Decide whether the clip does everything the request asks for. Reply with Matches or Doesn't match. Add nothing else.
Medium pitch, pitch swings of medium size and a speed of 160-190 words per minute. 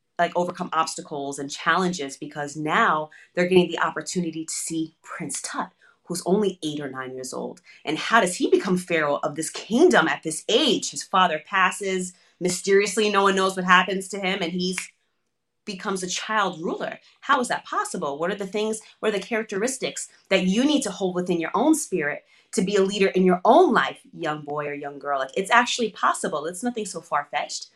Doesn't match